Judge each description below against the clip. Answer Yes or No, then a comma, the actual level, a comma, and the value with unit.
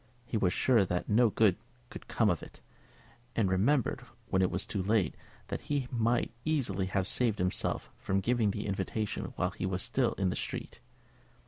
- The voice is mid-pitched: No, low, 105 Hz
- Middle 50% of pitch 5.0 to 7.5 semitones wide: No, average, 3.9 semitones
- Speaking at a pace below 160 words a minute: No, average, 185 wpm